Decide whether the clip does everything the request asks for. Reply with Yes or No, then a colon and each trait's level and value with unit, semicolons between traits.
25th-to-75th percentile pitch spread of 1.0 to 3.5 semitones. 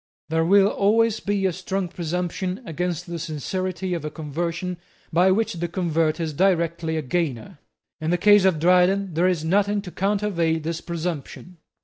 Yes: average, 2.7 semitones